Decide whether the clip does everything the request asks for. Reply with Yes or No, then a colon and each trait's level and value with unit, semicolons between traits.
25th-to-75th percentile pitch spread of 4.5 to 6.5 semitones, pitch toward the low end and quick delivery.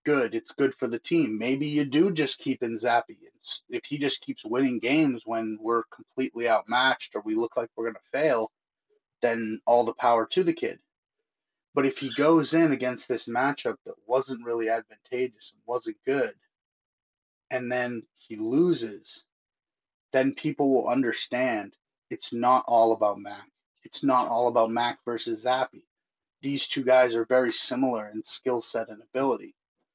No: wide, 5.4 semitones; low, 130 Hz; average, 170 wpm